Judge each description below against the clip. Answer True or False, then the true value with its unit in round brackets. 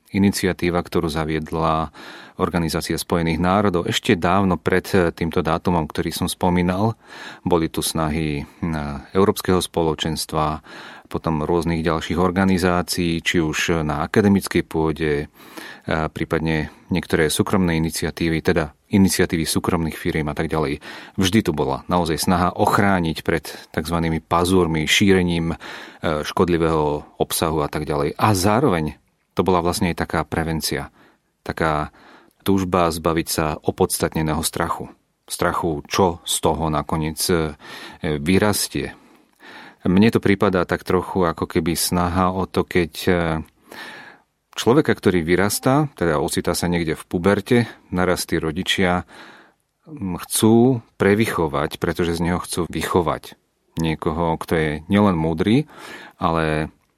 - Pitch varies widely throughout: False (2.6 semitones)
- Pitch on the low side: True (85 Hz)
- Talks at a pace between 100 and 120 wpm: True (115 wpm)